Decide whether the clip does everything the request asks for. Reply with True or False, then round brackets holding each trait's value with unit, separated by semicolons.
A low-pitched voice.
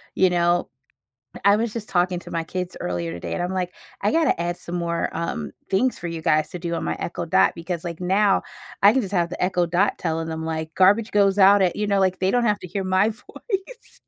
False (180 Hz)